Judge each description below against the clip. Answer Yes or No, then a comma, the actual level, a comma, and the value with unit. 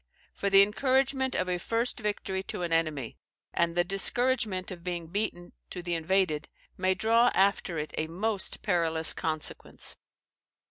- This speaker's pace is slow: No, average, 150 wpm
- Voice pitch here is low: No, medium, 185 Hz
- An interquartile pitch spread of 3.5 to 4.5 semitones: Yes, average, 3.9 semitones